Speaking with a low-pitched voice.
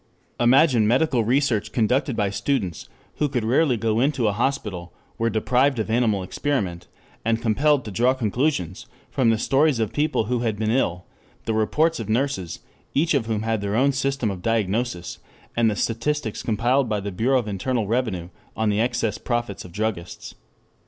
Yes: low, 115 Hz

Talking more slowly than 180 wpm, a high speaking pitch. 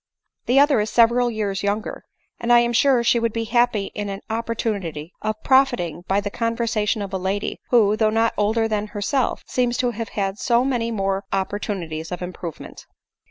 No: average, 195 wpm; high, 215 Hz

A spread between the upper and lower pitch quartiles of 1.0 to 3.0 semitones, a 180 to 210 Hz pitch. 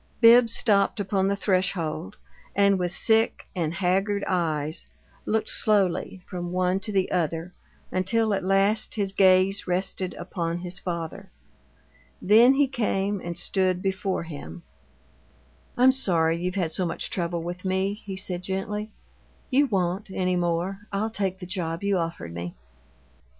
Yes: narrow, 2.5 semitones; high, 190 Hz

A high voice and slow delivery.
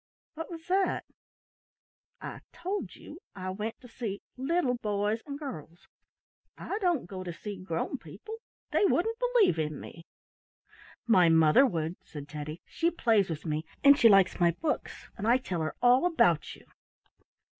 No: high, 220 Hz; average, 160 wpm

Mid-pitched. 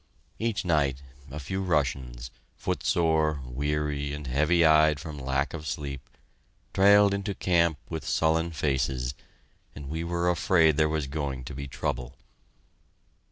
No: very low, 75 Hz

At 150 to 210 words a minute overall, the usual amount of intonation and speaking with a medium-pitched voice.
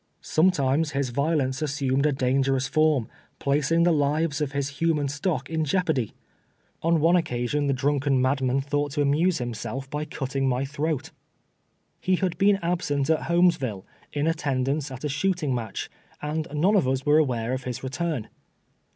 Yes: average, 165 wpm; average, 3.1 semitones; medium, 145 Hz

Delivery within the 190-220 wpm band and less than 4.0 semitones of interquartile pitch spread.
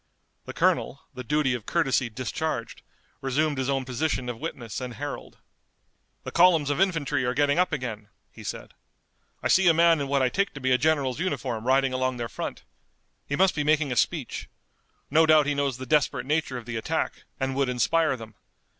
Yes: average, 200 wpm; average, 3.5 semitones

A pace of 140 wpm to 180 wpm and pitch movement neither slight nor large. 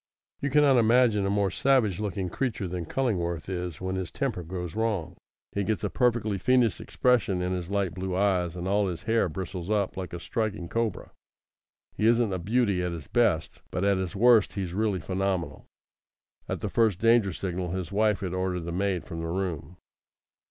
No: average, 190 wpm; average, 3.6 semitones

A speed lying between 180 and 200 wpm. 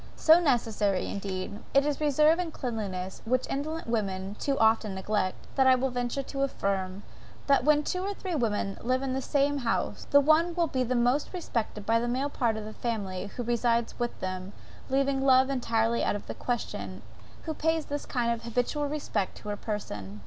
Yes: average, 190 wpm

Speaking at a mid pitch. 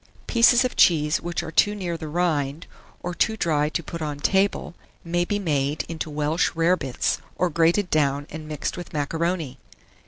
Yes: medium, 165 Hz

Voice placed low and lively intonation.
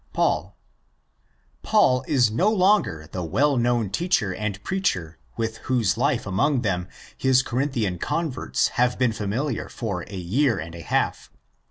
Yes: low, 120 Hz; wide, 5.9 semitones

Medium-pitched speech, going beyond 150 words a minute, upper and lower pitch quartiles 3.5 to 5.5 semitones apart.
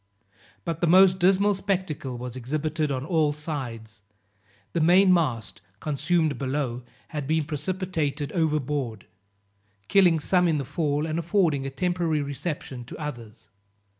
No: medium, 155 Hz; slow, 135 wpm; average, 4.2 semitones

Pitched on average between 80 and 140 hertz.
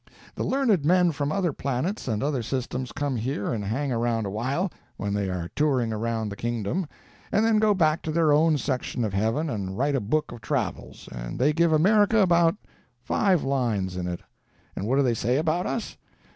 Yes: low, 135 Hz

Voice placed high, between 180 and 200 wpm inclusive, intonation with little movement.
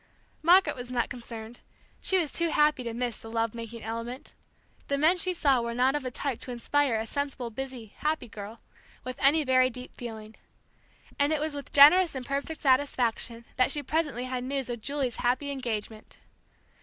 No: very high, 255 Hz; average, 185 wpm; average, 3.6 semitones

